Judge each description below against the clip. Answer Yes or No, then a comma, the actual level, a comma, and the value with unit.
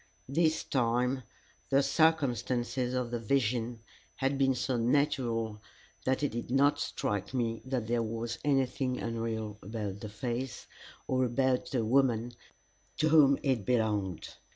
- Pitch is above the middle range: No, low, 125 Hz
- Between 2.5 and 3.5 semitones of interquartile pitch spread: Yes, average, 2.8 semitones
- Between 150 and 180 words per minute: No, slow, 135 wpm